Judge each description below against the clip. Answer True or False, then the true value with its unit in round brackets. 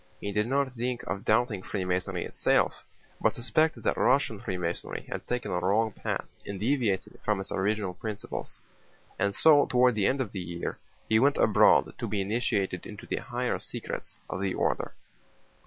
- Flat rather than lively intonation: False (4.3 semitones)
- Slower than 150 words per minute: False (170 wpm)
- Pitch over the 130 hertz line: False (105 Hz)